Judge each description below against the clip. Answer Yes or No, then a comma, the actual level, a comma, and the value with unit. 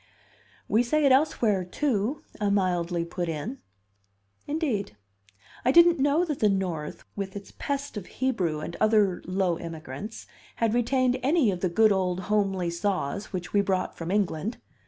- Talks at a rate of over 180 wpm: No, average, 155 wpm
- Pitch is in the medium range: No, high, 200 Hz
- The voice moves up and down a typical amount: No, wide, 5.7 semitones